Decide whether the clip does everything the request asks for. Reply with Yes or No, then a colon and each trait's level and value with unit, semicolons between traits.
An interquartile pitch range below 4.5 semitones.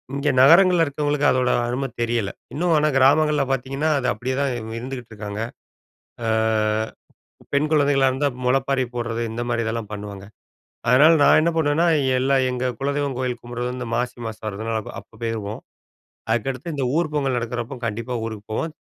Yes: average, 3.6 semitones